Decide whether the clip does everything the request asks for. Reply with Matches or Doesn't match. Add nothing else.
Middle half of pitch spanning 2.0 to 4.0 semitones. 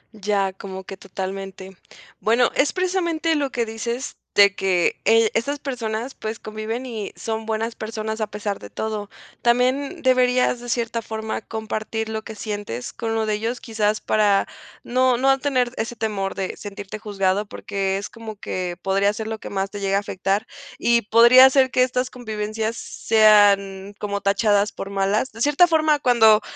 Matches